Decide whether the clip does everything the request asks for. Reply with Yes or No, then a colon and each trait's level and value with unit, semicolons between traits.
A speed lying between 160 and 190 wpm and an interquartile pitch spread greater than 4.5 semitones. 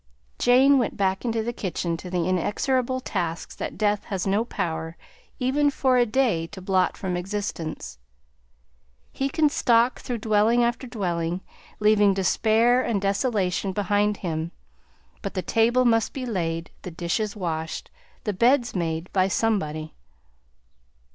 No: average, 140 wpm; average, 5.0 semitones